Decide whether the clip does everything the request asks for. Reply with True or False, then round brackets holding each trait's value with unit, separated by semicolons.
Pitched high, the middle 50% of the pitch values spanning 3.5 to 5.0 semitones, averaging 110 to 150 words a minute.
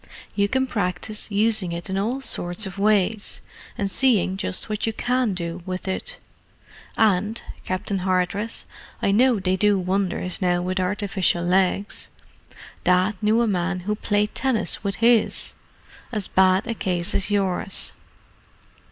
False (195 Hz; 2.7 semitones; 145 wpm)